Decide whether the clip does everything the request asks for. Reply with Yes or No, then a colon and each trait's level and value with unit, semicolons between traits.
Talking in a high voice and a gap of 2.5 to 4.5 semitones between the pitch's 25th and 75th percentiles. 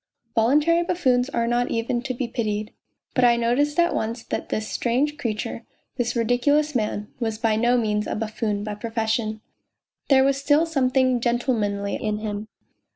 Yes: high, 235 Hz; average, 3.3 semitones